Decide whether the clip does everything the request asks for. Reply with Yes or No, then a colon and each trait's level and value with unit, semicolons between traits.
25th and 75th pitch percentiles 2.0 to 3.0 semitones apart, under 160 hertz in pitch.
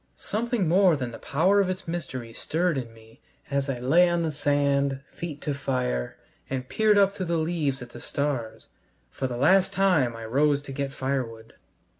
No: average, 5.2 semitones; medium, 140 Hz